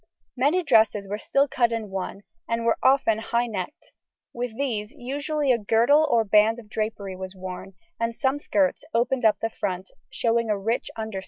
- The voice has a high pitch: Yes, high, 225 Hz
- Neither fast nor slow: Yes, average, 180 wpm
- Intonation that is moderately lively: Yes, average, 3.3 semitones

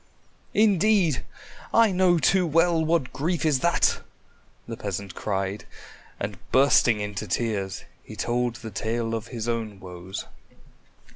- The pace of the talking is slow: Yes, slow, 130 wpm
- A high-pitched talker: No, low, 120 Hz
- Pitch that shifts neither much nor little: No, wide, 8.0 semitones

